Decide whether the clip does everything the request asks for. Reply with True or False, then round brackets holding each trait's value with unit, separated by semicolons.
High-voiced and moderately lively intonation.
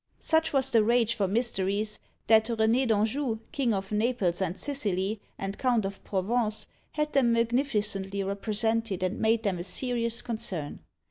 True (220 Hz; 3.4 semitones)